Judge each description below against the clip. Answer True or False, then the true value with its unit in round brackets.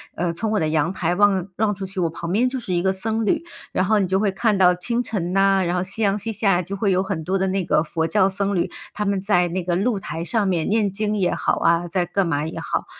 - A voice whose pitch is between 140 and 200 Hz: True (190 Hz)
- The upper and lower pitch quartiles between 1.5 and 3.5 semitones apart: True (2.7 semitones)